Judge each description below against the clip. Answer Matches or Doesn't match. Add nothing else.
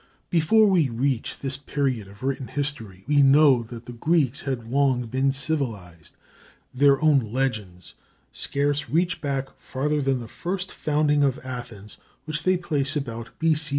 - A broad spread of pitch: Doesn't match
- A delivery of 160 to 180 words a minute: Doesn't match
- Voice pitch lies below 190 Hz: Matches